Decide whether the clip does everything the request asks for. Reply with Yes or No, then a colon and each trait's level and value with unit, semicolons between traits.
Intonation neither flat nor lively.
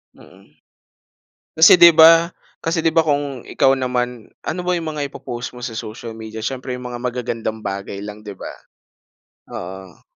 Yes: average, 5.0 semitones